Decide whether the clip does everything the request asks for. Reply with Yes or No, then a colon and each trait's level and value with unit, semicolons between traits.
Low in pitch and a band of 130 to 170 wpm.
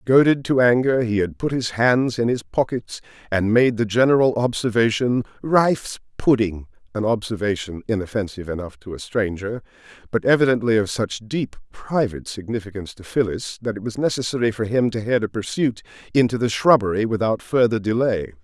Yes: low, 115 Hz; average, 160 wpm